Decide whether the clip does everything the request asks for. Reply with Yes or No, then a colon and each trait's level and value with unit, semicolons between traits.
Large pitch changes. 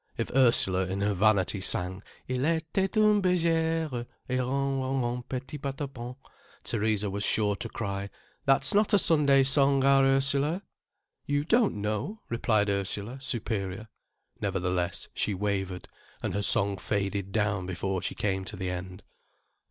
Yes: wide, 5.8 semitones